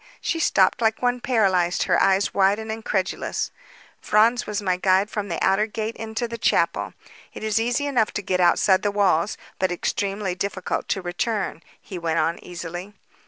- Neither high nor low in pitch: No, high, 200 Hz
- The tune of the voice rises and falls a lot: No, average, 3.0 semitones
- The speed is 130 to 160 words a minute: No, average, 175 wpm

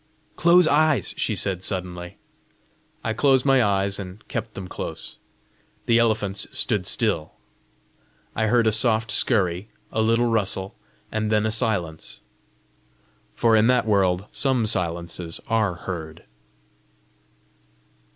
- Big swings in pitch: No, average, 3.8 semitones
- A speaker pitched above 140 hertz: No, low, 105 Hz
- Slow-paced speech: Yes, slow, 120 wpm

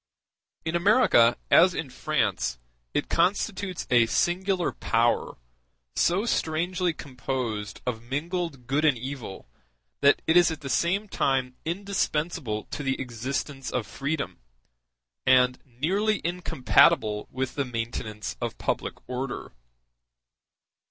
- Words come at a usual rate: No, slow, 115 wpm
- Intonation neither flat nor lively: No, wide, 5.9 semitones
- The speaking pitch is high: No, medium, 140 Hz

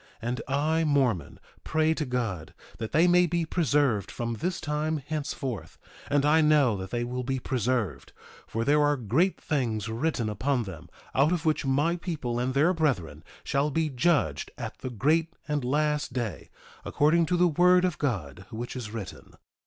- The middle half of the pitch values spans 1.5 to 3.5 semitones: No, average, 5.0 semitones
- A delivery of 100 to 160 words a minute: No, average, 175 wpm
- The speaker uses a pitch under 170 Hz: Yes, medium, 140 Hz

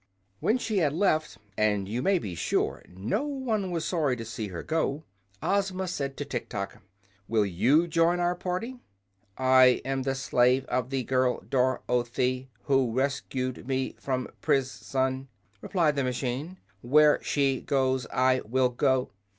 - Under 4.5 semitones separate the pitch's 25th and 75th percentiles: Yes, average, 4.0 semitones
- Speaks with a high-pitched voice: No, low, 130 Hz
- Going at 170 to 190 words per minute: No, average, 160 wpm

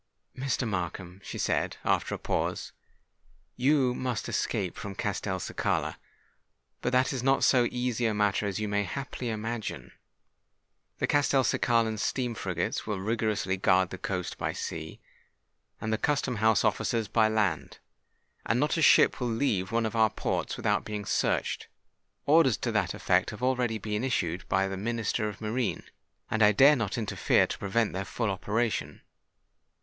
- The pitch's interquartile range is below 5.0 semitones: Yes, average, 3.6 semitones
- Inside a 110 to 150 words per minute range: No, average, 160 wpm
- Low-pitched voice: Yes, low, 110 Hz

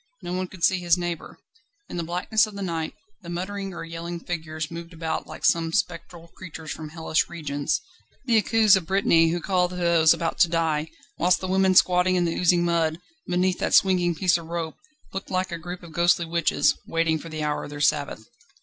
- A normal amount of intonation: No, narrow, 2.0 semitones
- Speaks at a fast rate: Yes, fast, 210 wpm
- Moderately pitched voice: Yes, medium, 170 Hz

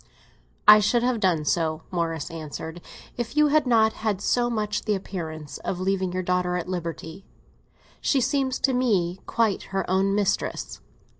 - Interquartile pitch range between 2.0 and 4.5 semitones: No, average, 4.9 semitones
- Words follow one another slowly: No, average, 160 wpm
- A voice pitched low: No, high, 195 Hz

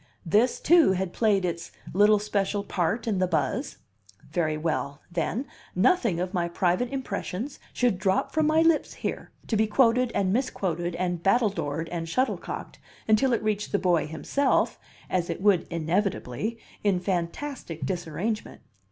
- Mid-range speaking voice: No, high, 195 Hz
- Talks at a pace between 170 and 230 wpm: No, average, 150 wpm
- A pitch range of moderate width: Yes, average, 4.9 semitones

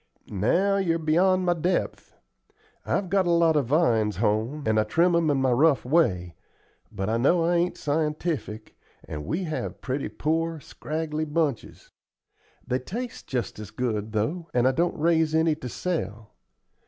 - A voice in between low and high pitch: Yes, medium, 155 Hz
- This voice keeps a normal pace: Yes, average, 165 wpm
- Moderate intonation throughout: No, wide, 6.2 semitones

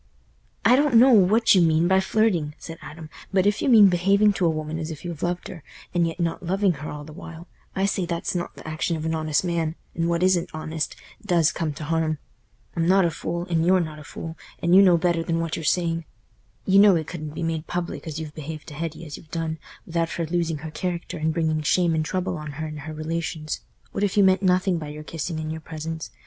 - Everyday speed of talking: No, fast, 245 wpm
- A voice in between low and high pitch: Yes, medium, 165 Hz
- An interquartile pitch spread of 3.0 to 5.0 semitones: No, narrow, 2.4 semitones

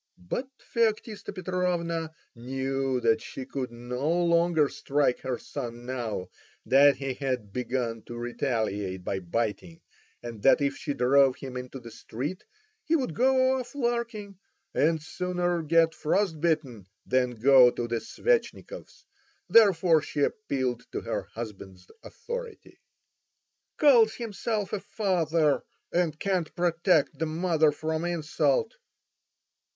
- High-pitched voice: No, medium, 155 Hz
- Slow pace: Yes, slow, 125 wpm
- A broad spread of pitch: Yes, wide, 6.5 semitones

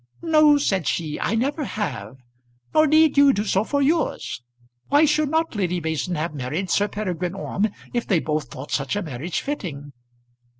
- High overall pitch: Yes, high, 200 Hz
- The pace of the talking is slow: No, average, 175 wpm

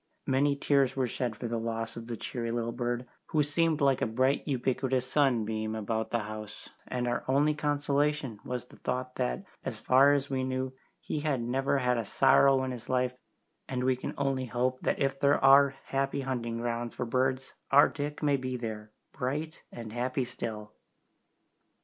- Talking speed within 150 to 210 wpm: Yes, average, 185 wpm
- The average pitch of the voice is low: Yes, low, 130 Hz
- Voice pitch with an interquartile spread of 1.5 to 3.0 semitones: Yes, average, 2.7 semitones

